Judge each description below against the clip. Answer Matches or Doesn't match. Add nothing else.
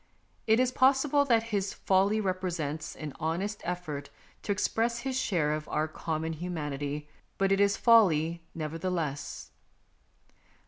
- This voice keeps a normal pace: Doesn't match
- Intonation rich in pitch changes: Matches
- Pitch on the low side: Doesn't match